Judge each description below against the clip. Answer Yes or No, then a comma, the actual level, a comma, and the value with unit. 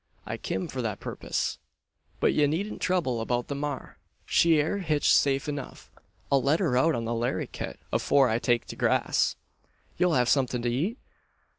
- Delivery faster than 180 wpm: No, average, 175 wpm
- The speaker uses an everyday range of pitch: Yes, average, 4.6 semitones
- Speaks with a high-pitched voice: No, medium, 140 Hz